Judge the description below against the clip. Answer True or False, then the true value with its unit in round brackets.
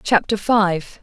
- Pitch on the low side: False (200 Hz)